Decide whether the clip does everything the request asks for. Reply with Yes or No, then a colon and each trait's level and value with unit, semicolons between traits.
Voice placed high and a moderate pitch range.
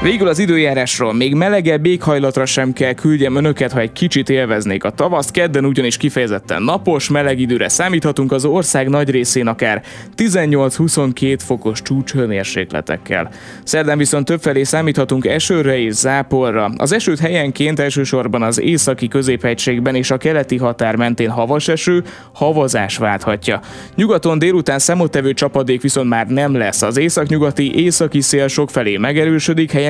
No: low, 135 Hz; average, 3.5 semitones